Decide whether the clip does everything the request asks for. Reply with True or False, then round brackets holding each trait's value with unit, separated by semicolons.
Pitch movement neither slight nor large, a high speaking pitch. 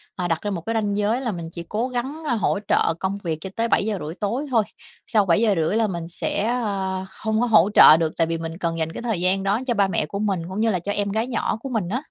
True (4.6 semitones; 200 Hz)